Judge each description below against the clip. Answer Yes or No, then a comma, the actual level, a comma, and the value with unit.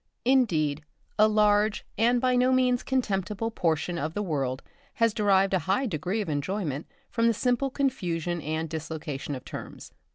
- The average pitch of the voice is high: Yes, high, 195 Hz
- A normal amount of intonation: No, wide, 6.4 semitones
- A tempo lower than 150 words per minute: No, average, 160 wpm